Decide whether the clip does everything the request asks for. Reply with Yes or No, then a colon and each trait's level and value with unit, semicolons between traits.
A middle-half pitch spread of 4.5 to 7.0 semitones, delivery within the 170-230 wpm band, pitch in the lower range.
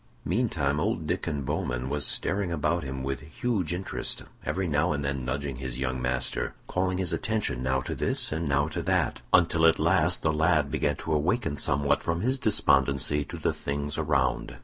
No: average, 3.9 semitones; average, 185 wpm; very low, 75 Hz